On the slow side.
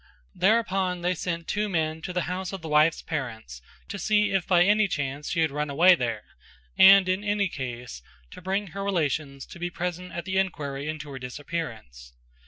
No: average, 190 wpm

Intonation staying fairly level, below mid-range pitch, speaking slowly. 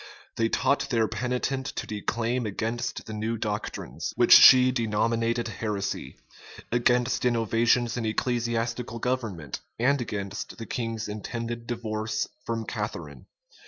Yes: narrow, 1.9 semitones; low, 115 Hz; slow, 120 wpm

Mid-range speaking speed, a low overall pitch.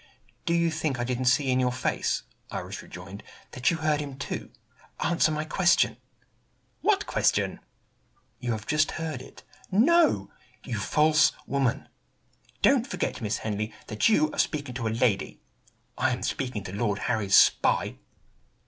Yes: average, 155 wpm; low, 130 Hz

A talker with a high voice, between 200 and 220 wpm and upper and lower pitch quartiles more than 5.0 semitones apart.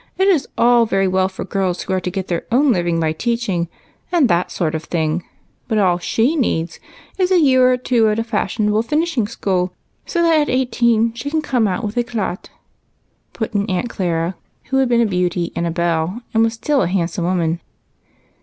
Yes: high, 210 Hz; fast, 205 wpm; wide, 5.5 semitones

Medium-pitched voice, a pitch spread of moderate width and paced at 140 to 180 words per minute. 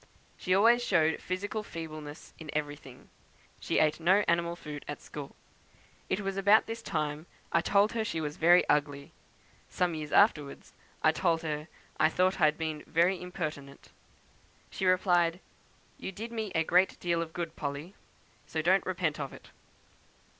Yes: medium, 170 Hz; average, 3.6 semitones; average, 160 wpm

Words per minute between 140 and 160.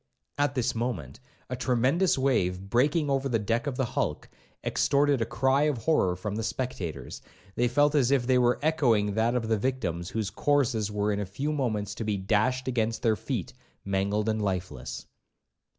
No: average, 185 wpm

